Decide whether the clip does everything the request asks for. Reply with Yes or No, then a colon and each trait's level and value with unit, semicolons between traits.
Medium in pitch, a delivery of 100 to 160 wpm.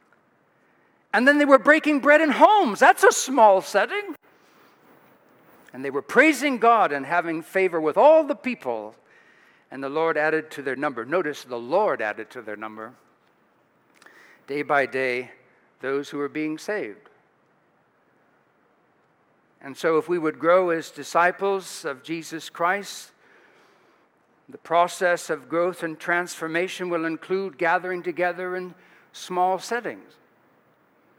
Yes: medium, 175 Hz; slow, 135 wpm